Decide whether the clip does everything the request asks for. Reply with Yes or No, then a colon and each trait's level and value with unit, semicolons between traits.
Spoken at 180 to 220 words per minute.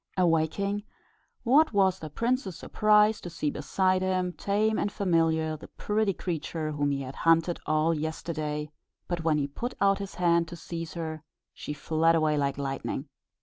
No: average, 165 wpm